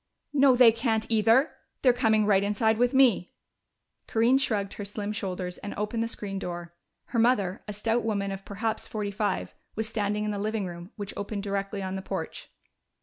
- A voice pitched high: Yes, high, 210 Hz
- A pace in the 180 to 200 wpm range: Yes, average, 190 wpm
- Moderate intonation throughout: No, narrow, 2.3 semitones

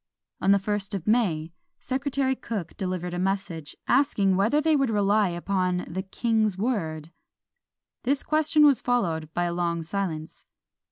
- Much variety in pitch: Yes, wide, 5.7 semitones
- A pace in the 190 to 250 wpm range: No, average, 150 wpm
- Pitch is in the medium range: No, high, 195 Hz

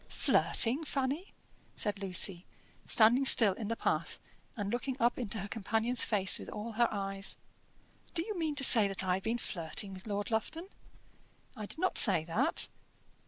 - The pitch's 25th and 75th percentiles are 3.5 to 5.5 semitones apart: Yes, average, 4.3 semitones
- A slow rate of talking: No, average, 170 wpm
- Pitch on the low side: No, high, 220 Hz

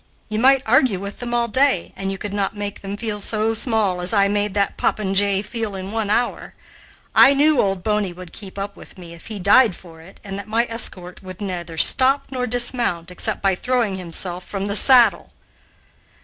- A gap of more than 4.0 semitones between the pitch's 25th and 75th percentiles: No, average, 3.3 semitones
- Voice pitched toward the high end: Yes, high, 205 Hz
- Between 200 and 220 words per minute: Yes, fast, 205 wpm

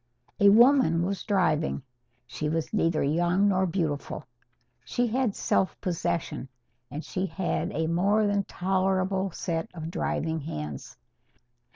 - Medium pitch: Yes, medium, 180 Hz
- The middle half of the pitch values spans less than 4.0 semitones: Yes, average, 3.5 semitones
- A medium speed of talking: No, slow, 130 wpm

